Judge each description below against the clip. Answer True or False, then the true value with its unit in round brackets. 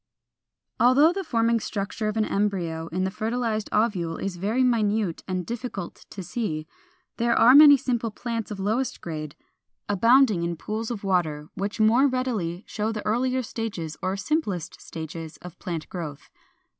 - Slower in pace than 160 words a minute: False (165 wpm)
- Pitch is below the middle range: False (210 Hz)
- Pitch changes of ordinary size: True (5.0 semitones)